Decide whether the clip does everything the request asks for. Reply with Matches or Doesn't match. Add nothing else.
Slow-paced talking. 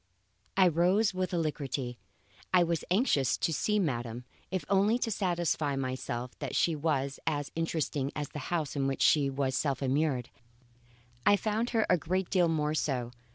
Doesn't match